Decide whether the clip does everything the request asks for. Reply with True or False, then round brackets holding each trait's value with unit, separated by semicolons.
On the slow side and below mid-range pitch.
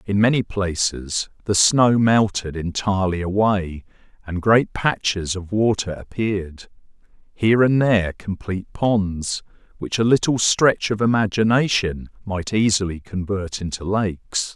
True (125 wpm; 100 Hz)